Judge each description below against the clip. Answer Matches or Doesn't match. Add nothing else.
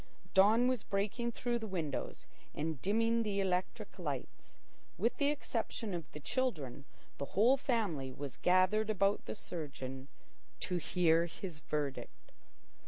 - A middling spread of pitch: Doesn't match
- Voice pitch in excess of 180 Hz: Matches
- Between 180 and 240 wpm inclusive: Doesn't match